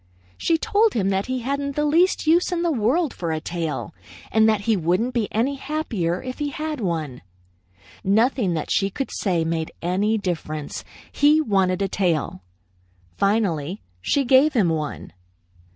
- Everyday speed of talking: Yes, average, 165 wpm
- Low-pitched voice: No, high, 215 Hz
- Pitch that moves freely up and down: Yes, wide, 8.2 semitones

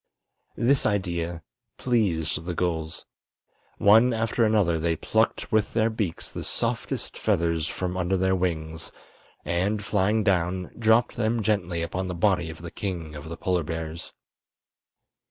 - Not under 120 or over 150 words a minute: Yes, average, 140 wpm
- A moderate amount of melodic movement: Yes, average, 4.2 semitones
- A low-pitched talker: Yes, very low, 90 Hz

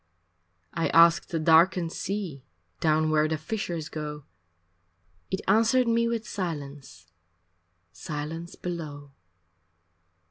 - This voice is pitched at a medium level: Yes, medium, 165 Hz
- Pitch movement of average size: Yes, average, 3.8 semitones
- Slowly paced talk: Yes, slow, 100 wpm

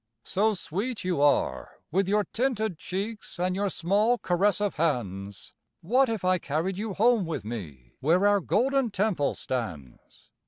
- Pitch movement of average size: No, wide, 6.2 semitones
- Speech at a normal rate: Yes, average, 150 wpm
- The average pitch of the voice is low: No, medium, 185 Hz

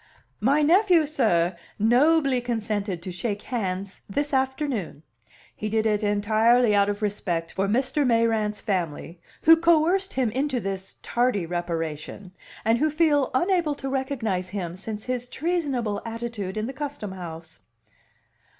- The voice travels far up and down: Yes, wide, 5.7 semitones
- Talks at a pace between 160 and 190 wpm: No, average, 140 wpm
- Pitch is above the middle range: Yes, high, 225 Hz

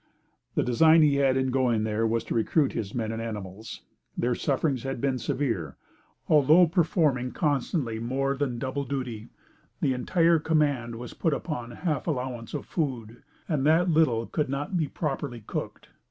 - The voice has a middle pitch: No, low, 130 Hz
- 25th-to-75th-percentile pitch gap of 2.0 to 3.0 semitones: No, average, 4.4 semitones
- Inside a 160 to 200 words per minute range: Yes, average, 165 wpm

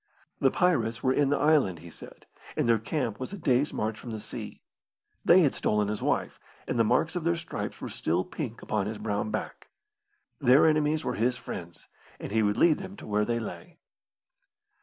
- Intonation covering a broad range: Yes, wide, 6.2 semitones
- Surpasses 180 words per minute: Yes, average, 200 wpm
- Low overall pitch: Yes, low, 120 Hz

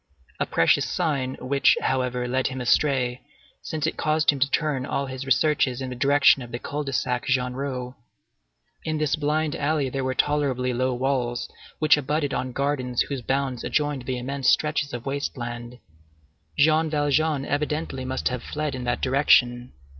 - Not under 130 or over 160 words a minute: No, average, 170 wpm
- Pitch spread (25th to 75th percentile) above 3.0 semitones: No, narrow, 2.6 semitones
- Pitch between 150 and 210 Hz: No, low, 135 Hz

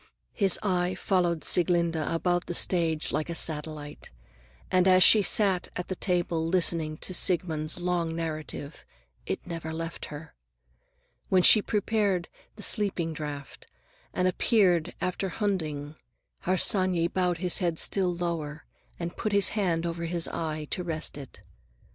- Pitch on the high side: No, medium, 175 Hz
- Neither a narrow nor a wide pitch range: No, narrow, 2.3 semitones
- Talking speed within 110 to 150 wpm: Yes, average, 140 wpm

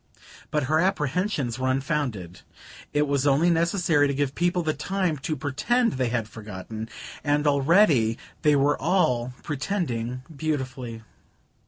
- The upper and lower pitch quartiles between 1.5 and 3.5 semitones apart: No, average, 4.3 semitones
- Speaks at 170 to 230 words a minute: No, slow, 135 wpm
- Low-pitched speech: No, medium, 145 Hz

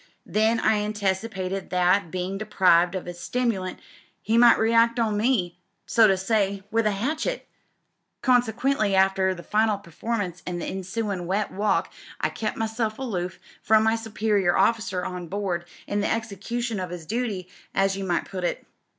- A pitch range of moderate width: Yes, average, 3.3 semitones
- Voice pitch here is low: No, high, 205 Hz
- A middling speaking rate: Yes, average, 165 wpm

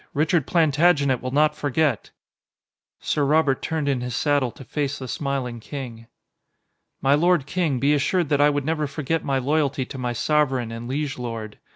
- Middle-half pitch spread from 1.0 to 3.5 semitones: Yes, average, 2.8 semitones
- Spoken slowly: No, average, 175 wpm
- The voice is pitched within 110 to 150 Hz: Yes, medium, 140 Hz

